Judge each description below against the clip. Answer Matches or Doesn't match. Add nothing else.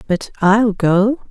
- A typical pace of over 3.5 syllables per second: Doesn't match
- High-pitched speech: Matches